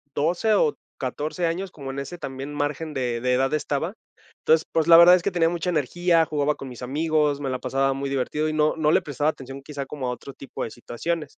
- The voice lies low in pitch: No, medium, 150 Hz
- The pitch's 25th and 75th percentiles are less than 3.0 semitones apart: No, average, 3.4 semitones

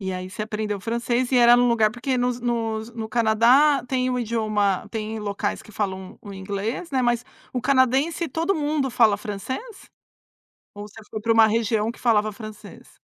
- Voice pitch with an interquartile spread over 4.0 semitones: No, average, 2.9 semitones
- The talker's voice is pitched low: No, high, 230 Hz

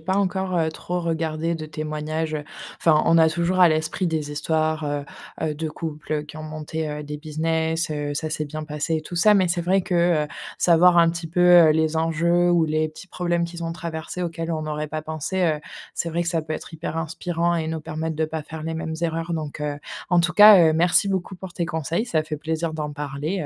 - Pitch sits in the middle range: Yes, medium, 160 Hz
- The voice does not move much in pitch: Yes, narrow, 1.7 semitones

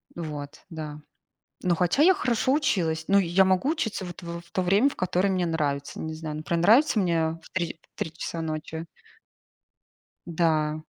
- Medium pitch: Yes, medium, 170 Hz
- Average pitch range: Yes, average, 3.2 semitones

